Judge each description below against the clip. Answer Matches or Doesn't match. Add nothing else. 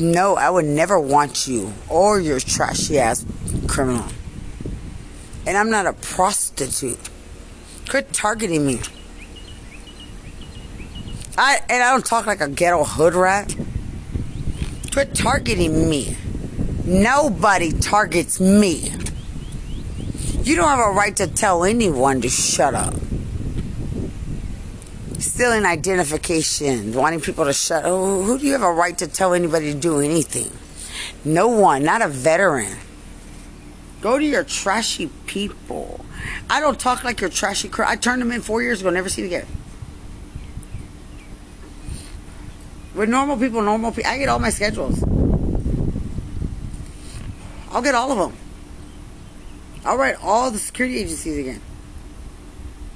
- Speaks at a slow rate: Matches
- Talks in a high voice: Doesn't match